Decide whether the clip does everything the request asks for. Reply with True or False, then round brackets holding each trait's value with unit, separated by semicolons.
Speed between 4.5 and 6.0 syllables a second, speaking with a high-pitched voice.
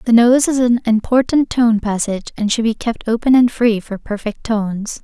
True (5.0 syllables/s; 230 Hz)